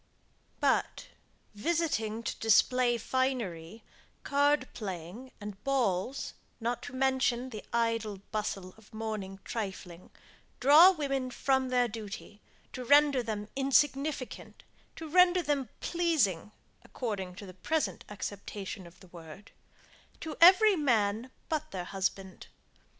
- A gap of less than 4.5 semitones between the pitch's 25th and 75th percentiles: No, average, 5.3 semitones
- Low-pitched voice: No, high, 235 Hz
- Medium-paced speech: No, slow, 115 wpm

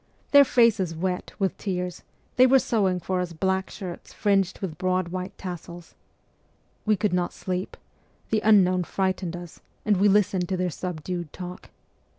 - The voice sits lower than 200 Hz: Yes, medium, 185 Hz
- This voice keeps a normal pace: Yes, average, 160 wpm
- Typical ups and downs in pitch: No, narrow, 1.8 semitones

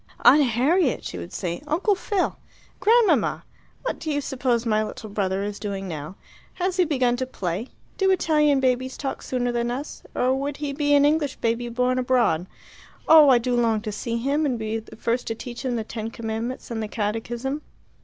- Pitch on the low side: No, high, 245 Hz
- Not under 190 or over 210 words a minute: Yes, average, 195 wpm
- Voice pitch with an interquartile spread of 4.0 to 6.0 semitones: Yes, average, 4.4 semitones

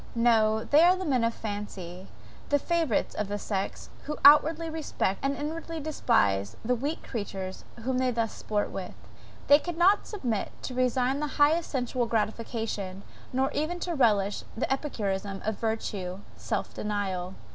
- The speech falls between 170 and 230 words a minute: No, average, 155 wpm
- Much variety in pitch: Yes, wide, 6.2 semitones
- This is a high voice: Yes, high, 235 Hz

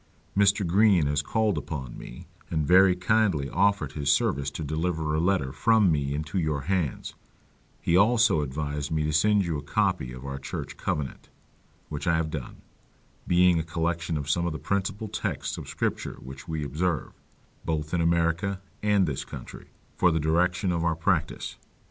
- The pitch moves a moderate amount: Yes, average, 3.9 semitones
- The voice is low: Yes, very low, 80 Hz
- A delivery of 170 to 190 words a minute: Yes, average, 175 wpm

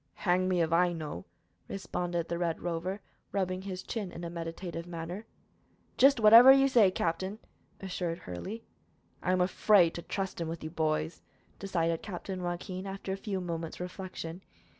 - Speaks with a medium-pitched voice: Yes, medium, 180 Hz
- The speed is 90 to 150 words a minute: No, average, 160 wpm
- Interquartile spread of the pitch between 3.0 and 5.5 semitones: No, narrow, 2.4 semitones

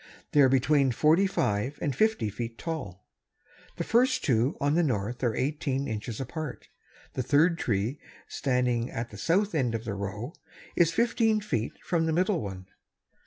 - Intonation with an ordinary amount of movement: No, wide, 6.0 semitones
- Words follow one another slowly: No, average, 165 wpm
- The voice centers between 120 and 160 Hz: Yes, low, 135 Hz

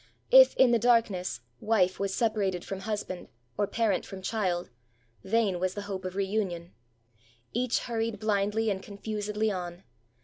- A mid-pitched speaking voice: No, high, 205 Hz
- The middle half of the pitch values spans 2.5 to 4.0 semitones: Yes, average, 2.9 semitones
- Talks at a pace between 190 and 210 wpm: No, average, 160 wpm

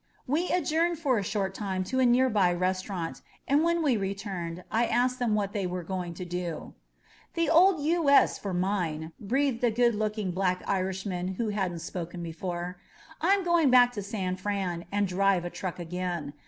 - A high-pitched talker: Yes, high, 195 Hz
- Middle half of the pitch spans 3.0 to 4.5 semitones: No, wide, 5.4 semitones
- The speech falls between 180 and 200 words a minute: Yes, average, 185 wpm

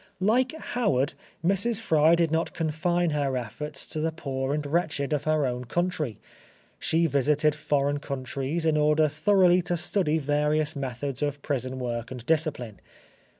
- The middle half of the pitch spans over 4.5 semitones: No, average, 3.0 semitones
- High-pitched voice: No, medium, 150 Hz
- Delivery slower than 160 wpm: Yes, average, 150 wpm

